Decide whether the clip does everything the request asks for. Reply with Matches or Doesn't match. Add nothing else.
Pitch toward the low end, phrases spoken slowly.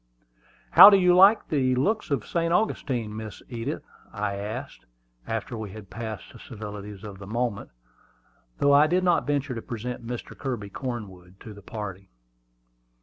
Doesn't match